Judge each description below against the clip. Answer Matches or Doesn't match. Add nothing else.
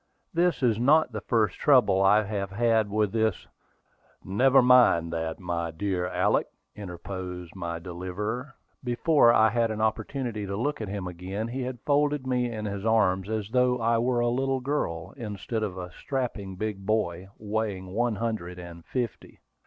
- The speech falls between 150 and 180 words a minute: Matches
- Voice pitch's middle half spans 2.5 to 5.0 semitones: Matches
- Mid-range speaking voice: Doesn't match